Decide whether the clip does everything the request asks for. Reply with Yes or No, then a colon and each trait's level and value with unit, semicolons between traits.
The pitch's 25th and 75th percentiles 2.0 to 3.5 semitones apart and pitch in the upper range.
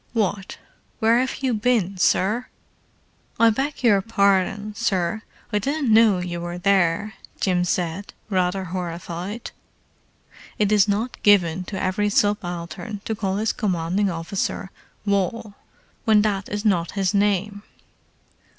Yes: average, 2.9 semitones; high, 200 Hz